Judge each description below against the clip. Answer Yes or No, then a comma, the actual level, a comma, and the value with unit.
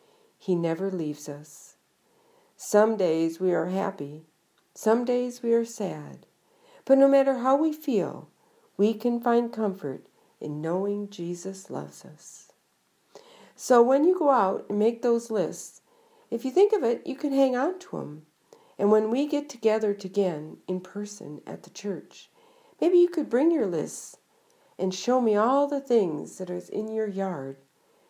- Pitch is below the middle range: No, high, 225 Hz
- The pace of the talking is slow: No, average, 165 wpm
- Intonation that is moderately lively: No, wide, 7.4 semitones